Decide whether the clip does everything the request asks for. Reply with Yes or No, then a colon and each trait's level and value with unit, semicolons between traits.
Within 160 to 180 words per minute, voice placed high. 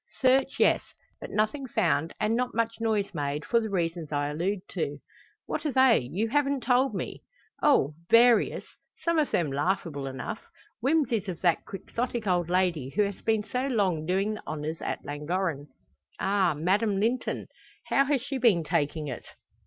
Yes: average, 170 wpm; high, 200 Hz